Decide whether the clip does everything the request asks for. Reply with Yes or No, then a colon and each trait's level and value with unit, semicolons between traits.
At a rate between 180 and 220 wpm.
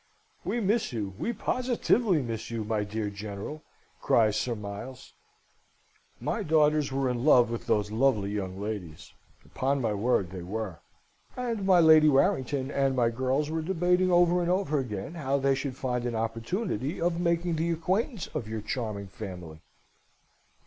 No: average, 160 wpm